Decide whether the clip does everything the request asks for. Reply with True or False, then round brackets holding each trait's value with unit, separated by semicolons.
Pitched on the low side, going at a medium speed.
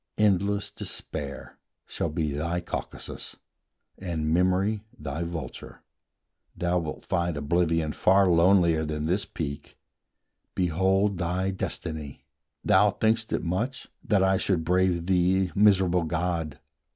False (90 Hz; 115 wpm)